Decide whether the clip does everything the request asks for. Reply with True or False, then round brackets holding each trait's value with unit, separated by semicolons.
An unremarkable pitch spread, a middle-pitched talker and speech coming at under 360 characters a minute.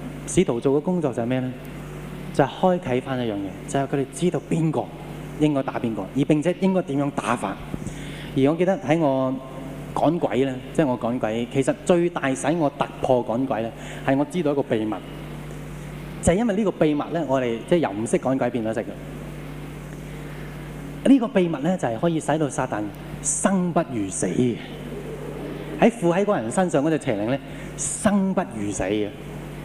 True (3.6 semitones; 145 Hz; 270 characters per minute)